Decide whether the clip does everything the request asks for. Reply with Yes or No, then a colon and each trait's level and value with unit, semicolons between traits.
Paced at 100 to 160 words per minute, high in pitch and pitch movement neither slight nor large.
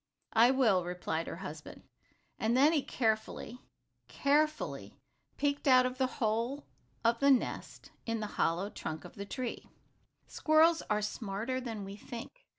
Yes: average, 150 wpm; high, 235 Hz; average, 4.6 semitones